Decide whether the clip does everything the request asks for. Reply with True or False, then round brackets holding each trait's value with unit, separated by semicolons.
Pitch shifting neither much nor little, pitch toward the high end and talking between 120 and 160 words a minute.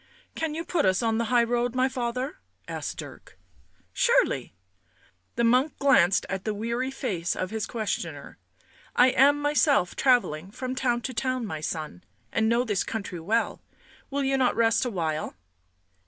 False (4.2 semitones; 240 Hz; 175 wpm)